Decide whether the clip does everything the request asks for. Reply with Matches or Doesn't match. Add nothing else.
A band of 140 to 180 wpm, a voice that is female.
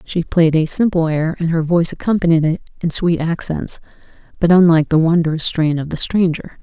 Doesn't match